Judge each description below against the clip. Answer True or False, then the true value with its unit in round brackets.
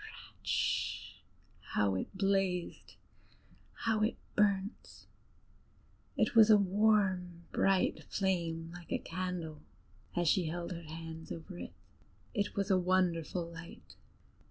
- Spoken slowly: True (115 wpm)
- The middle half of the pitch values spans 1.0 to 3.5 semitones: True (2.8 semitones)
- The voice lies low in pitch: False (180 Hz)